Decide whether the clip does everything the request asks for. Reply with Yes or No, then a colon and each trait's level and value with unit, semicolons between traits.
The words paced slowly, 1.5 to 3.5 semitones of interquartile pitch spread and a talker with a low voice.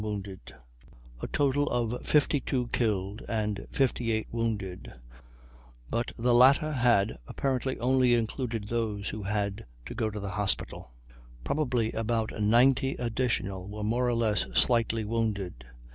Yes: slow, 130 wpm; average, 2.9 semitones; low, 115 Hz